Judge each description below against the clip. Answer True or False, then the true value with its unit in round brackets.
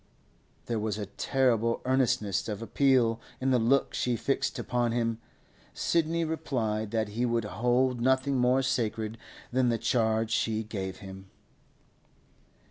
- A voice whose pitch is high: False (115 Hz)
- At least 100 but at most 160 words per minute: True (135 wpm)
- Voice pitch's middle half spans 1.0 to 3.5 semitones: True (2.9 semitones)